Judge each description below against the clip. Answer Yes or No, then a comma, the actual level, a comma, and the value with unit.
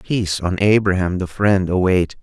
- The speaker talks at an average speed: Yes, average, 160 wpm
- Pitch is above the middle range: No, very low, 95 Hz